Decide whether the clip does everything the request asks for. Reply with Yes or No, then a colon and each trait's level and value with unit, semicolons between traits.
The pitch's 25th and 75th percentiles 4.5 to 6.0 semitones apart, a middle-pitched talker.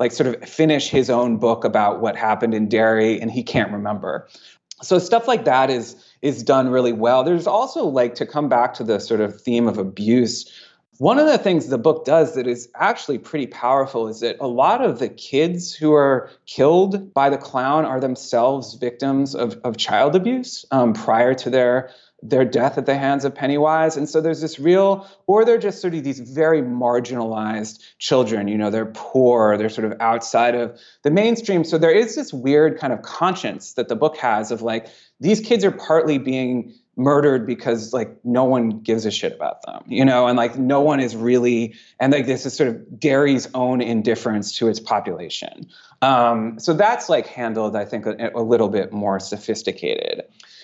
No: average, 4.8 semitones; low, 130 Hz